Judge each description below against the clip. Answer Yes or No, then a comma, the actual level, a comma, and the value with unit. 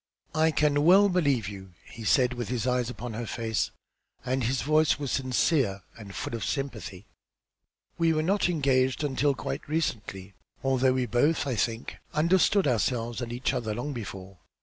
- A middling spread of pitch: Yes, average, 4.4 semitones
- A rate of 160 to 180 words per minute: Yes, average, 170 wpm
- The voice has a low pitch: Yes, low, 130 Hz